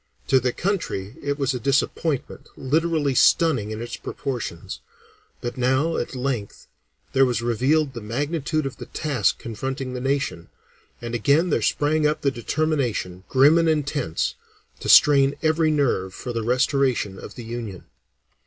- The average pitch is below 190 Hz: Yes, low, 135 Hz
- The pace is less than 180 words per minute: Yes, average, 155 wpm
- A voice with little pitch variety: No, average, 4.0 semitones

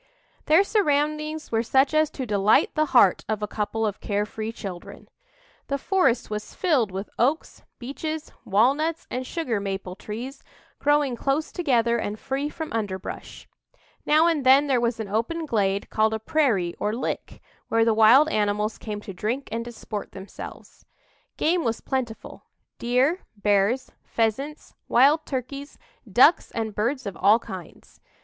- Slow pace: No, average, 155 wpm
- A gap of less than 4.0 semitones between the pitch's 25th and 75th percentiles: No, wide, 5.5 semitones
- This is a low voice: No, high, 235 Hz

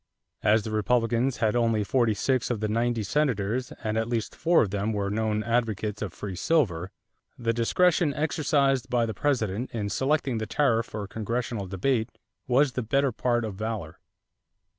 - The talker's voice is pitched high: No, low, 115 Hz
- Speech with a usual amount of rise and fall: Yes, average, 3.1 semitones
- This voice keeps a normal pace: Yes, average, 170 wpm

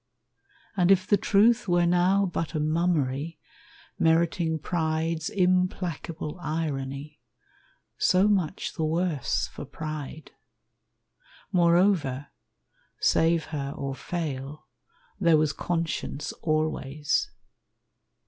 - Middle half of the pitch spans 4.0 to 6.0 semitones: No, average, 2.8 semitones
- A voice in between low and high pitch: Yes, medium, 160 Hz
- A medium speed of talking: No, slow, 90 wpm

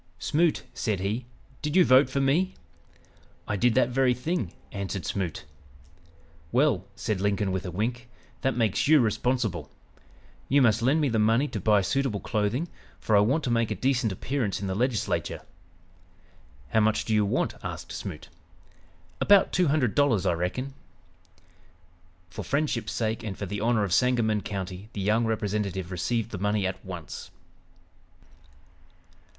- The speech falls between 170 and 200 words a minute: No, average, 155 wpm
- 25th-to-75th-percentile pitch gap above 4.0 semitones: Yes, average, 4.4 semitones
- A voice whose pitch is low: Yes, low, 110 Hz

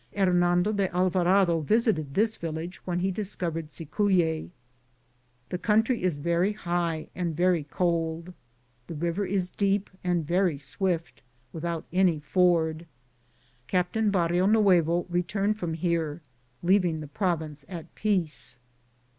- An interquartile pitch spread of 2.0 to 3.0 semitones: Yes, narrow, 2.6 semitones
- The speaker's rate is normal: No, slow, 125 wpm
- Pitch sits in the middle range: Yes, medium, 175 Hz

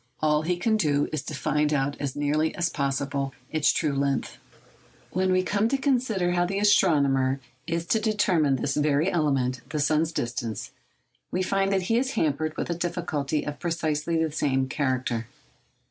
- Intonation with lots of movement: No, average, 4.1 semitones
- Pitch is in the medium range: Yes, medium, 155 Hz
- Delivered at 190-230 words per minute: No, average, 165 wpm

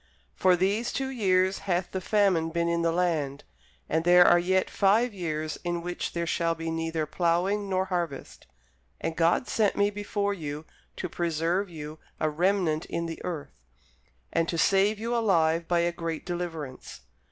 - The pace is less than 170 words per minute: No, average, 175 wpm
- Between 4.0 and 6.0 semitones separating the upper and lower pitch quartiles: No, average, 2.9 semitones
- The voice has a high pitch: No, medium, 175 Hz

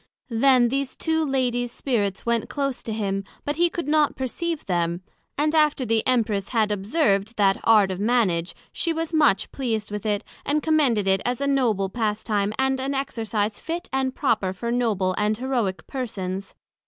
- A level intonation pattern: No, average, 5.1 semitones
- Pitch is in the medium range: No, high, 235 Hz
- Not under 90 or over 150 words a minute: No, average, 175 wpm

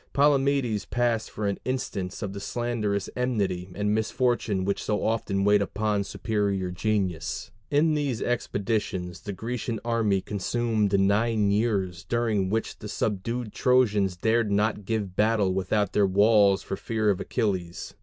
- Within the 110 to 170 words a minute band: Yes, average, 145 wpm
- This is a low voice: Yes, low, 105 Hz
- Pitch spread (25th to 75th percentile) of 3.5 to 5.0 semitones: No, average, 2.9 semitones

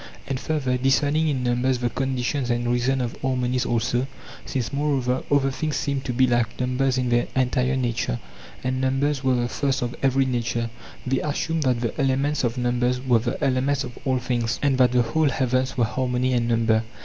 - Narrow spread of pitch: Yes, narrow, 1.6 semitones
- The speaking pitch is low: Yes, low, 130 Hz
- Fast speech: No, average, 195 wpm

